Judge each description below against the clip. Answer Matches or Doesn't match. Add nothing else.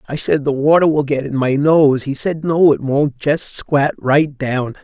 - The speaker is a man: Matches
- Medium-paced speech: Doesn't match